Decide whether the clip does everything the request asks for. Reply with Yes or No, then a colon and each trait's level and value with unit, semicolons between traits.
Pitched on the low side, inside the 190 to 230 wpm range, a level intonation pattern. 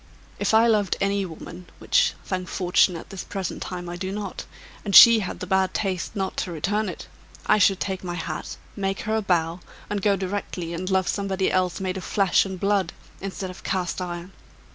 No: high, 190 Hz; fast, 205 wpm; narrow, 1.8 semitones